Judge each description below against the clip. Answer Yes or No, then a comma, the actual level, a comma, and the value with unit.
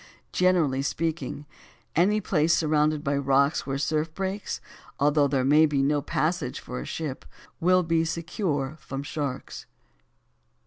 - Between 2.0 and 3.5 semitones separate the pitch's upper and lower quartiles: Yes, average, 3.1 semitones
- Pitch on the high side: No, medium, 150 Hz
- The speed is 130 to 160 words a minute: Yes, average, 140 wpm